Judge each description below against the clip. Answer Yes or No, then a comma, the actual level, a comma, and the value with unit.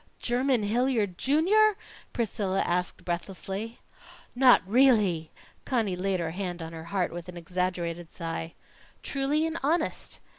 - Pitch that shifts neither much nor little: No, wide, 6.7 semitones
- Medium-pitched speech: No, high, 195 Hz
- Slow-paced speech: Yes, slow, 125 wpm